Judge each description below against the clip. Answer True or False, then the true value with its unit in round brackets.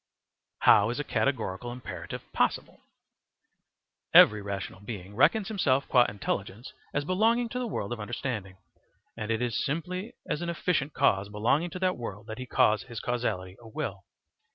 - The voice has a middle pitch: False (120 Hz)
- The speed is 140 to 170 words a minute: True (160 wpm)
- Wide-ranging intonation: True (7.1 semitones)